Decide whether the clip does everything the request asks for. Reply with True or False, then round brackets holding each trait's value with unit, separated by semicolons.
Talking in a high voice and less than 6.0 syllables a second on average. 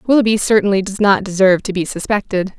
False (200 Hz; 6.3 syllables/s)